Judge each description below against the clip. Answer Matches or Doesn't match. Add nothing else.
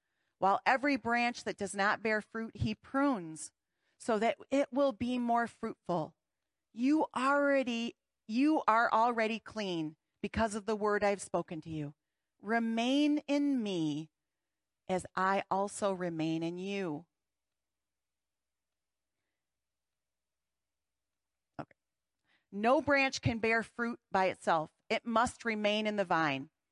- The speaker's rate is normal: Doesn't match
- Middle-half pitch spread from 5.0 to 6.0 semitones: Matches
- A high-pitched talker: Matches